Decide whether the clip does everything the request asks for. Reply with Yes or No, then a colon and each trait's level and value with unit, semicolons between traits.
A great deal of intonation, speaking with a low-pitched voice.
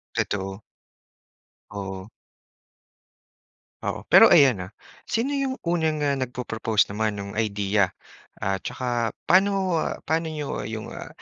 Yes: wide, 8.0 semitones; low, 115 Hz